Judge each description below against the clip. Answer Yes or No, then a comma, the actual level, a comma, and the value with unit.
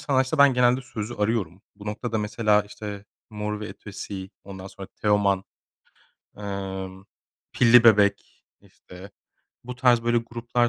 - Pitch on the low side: Yes, low, 105 Hz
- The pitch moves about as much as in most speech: Yes, average, 3.1 semitones